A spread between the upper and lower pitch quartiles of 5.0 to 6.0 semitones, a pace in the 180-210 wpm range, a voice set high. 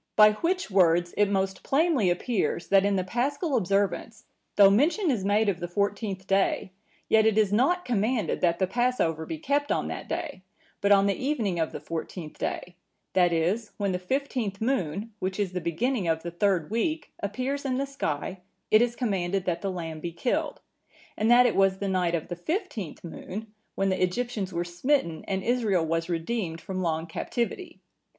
Yes: wide, 5.4 semitones; average, 190 wpm; high, 200 Hz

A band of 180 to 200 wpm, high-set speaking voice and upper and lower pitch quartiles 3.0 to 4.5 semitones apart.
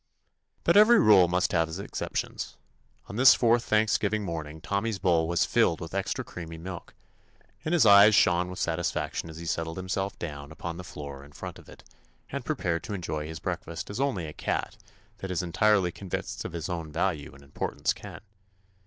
No: average, 195 wpm; very low, 90 Hz; average, 3.6 semitones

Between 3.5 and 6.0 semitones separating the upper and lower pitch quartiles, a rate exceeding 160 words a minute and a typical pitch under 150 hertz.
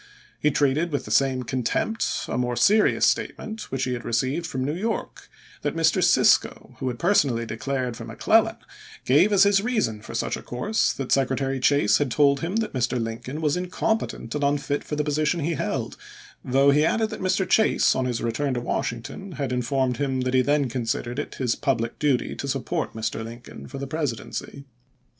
Yes: average, 3.8 semitones; average, 190 wpm; medium, 140 Hz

